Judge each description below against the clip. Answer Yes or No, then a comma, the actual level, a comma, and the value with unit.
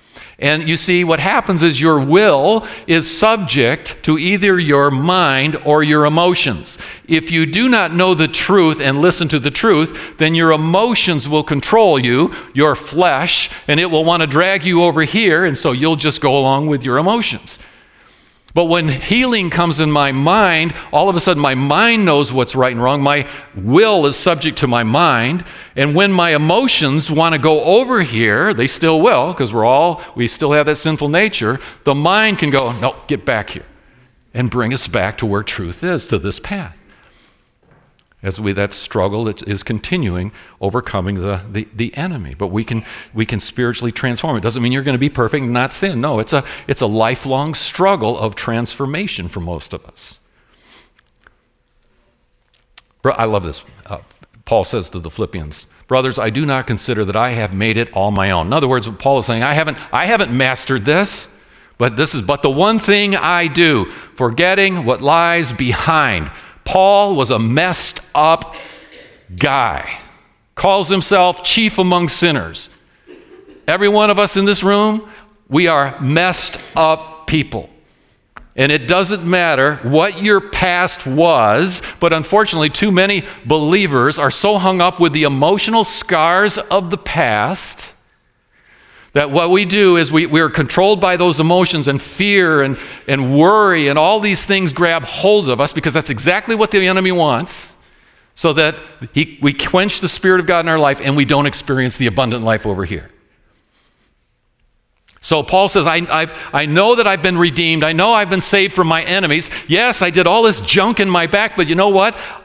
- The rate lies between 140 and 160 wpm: No, average, 185 wpm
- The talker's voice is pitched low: No, medium, 155 Hz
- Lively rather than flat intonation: Yes, wide, 5.8 semitones